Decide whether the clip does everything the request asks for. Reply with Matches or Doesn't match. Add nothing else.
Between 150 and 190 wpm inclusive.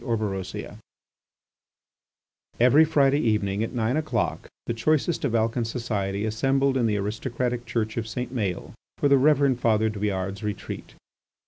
Doesn't match